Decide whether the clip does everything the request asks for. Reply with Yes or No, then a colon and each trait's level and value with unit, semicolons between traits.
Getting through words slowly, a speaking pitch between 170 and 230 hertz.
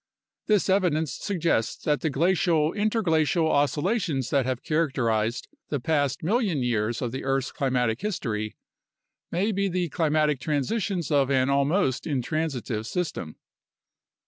No: slow, 125 wpm; medium, 150 Hz